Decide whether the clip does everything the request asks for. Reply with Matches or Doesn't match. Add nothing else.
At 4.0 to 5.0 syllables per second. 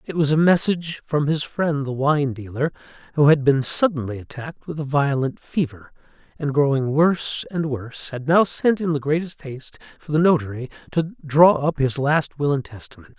Doesn't match